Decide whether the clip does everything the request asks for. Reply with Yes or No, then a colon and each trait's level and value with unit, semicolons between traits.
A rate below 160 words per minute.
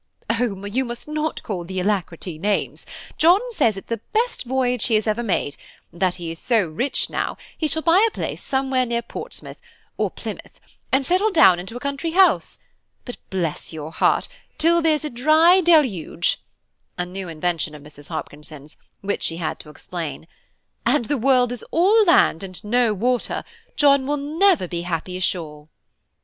No: average, 175 wpm